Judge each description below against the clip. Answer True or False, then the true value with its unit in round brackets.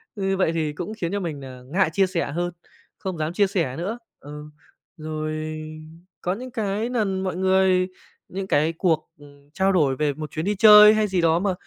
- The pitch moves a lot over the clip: False (4.0 semitones)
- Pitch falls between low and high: True (180 Hz)